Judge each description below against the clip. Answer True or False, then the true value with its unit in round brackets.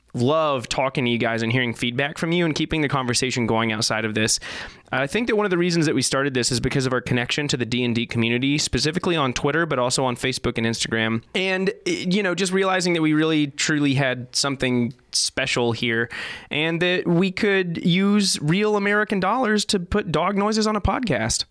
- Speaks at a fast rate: True (210 wpm)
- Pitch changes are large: True (6.5 semitones)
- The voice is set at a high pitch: False (145 Hz)